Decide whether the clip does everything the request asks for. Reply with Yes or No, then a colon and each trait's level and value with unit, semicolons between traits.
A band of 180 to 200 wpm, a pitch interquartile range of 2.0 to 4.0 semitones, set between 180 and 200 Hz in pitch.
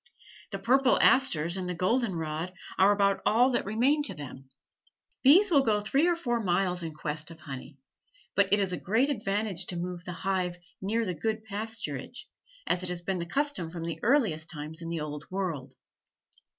No: average, 190 wpm; average, 5.2 semitones; high, 190 Hz